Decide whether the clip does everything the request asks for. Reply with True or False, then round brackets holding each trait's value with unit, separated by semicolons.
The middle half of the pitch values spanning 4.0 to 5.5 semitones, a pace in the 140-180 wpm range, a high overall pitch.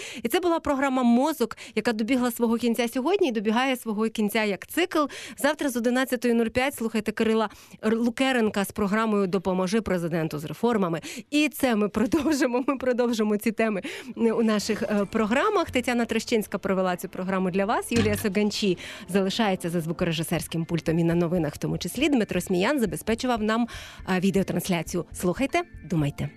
True (4.8 semitones; 150 wpm; 220 Hz)